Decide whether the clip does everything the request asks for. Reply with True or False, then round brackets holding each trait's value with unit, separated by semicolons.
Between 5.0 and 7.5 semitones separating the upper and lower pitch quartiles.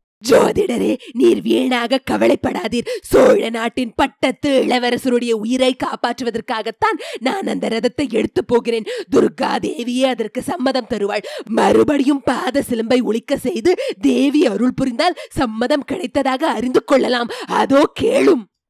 False (3.4 semitones)